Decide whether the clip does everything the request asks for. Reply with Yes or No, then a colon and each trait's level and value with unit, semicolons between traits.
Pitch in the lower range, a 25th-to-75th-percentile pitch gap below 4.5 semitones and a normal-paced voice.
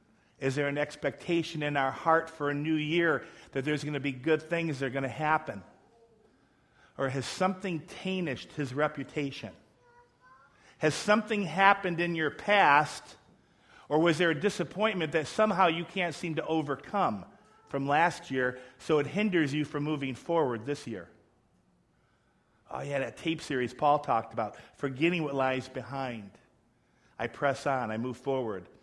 No: medium, 150 Hz; average, 3.8 semitones; average, 160 wpm